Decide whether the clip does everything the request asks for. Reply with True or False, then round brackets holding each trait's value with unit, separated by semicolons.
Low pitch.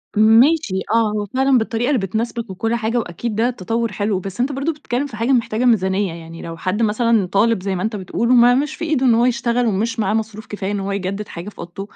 False (220 Hz)